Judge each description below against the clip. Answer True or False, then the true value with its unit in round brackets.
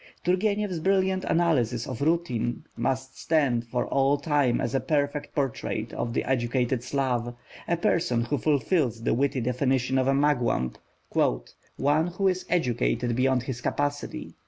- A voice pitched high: False (135 Hz)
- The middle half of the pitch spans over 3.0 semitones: True (4.3 semitones)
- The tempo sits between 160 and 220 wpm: False (145 wpm)